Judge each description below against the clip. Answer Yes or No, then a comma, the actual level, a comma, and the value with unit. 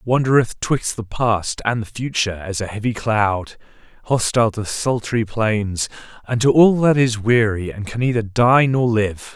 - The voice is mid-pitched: No, low, 115 Hz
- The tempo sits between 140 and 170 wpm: Yes, average, 165 wpm